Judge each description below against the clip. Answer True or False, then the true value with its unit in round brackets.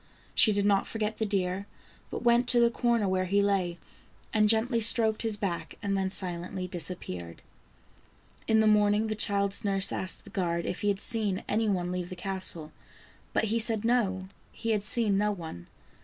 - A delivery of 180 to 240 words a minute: True (185 wpm)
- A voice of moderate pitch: False (200 Hz)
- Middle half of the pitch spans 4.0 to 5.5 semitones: False (2.9 semitones)